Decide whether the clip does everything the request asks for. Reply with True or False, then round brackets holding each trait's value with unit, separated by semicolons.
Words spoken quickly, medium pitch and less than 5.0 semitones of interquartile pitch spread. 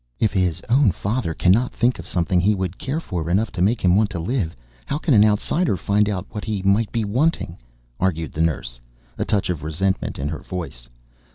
False (210 wpm; 95 Hz; 4.2 semitones)